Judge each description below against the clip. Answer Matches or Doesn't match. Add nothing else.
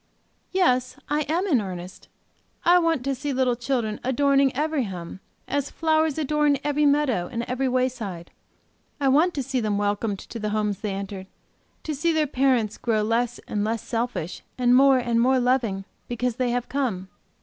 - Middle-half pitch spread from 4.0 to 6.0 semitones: Matches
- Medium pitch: Doesn't match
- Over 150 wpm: Matches